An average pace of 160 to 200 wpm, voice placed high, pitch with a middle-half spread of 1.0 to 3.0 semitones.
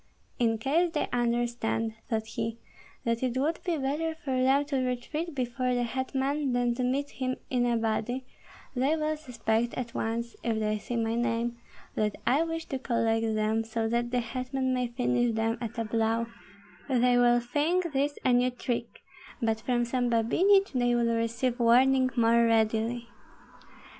Yes: average, 170 wpm; high, 245 Hz; narrow, 2.4 semitones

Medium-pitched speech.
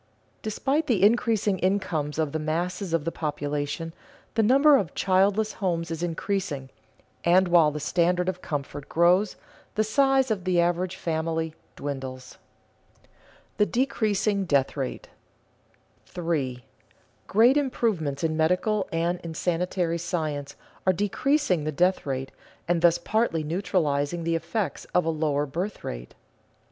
Yes: medium, 175 Hz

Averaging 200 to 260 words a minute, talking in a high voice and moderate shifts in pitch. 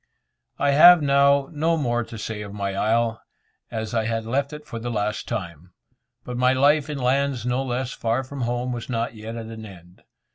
No: fast, 205 wpm; low, 120 Hz; average, 3.9 semitones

